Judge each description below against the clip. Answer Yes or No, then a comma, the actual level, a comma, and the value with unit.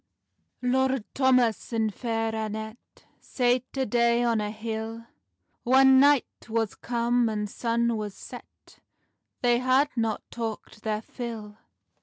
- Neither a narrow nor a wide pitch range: No, narrow, 2.2 semitones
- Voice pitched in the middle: No, high, 235 Hz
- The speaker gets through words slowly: Yes, slow, 130 wpm